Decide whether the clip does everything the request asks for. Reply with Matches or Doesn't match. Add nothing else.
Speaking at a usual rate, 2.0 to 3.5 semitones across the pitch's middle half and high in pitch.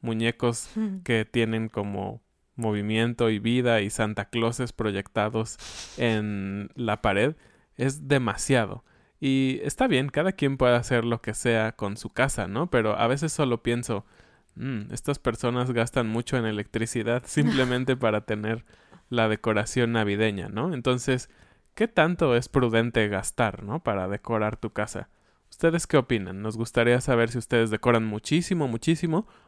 Doesn't match